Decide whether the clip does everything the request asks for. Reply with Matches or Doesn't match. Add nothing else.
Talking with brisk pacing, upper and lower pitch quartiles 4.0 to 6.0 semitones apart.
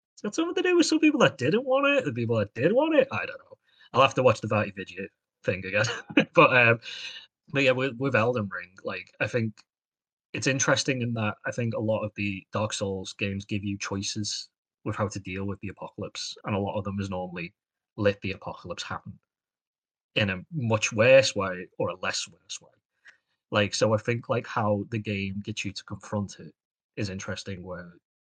Matches